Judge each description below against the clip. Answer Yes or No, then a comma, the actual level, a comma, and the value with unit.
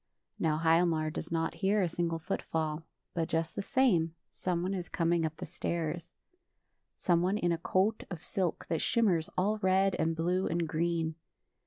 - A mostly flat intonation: Yes, narrow, 2.3 semitones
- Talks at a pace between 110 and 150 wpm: No, average, 175 wpm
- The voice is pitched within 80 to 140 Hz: No, medium, 170 Hz